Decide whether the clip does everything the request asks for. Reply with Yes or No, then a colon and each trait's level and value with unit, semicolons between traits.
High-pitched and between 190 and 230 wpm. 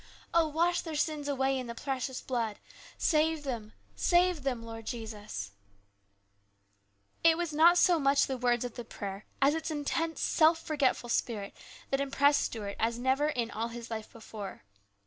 No: very high, 265 Hz; average, 165 wpm